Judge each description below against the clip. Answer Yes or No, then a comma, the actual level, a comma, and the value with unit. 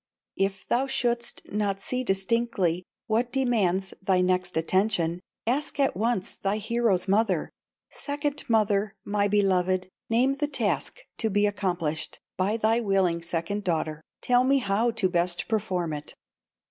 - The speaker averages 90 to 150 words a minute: Yes, average, 140 wpm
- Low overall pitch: No, high, 205 Hz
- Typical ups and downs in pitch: Yes, average, 4.2 semitones